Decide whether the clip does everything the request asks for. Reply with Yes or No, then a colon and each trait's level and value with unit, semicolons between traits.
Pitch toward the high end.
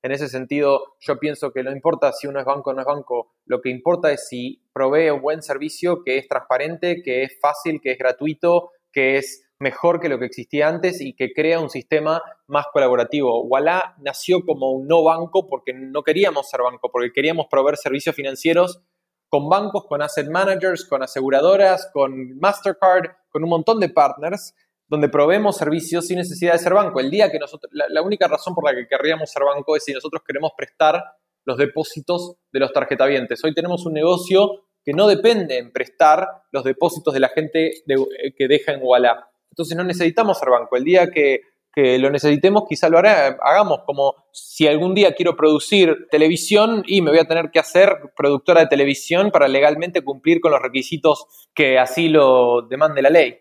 No: medium, 155 Hz